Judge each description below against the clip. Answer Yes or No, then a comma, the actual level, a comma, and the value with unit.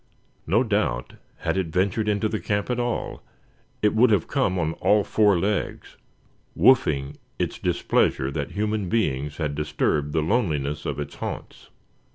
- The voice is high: No, low, 100 Hz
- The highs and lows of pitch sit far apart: Yes, wide, 6.3 semitones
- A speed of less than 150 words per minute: No, average, 155 wpm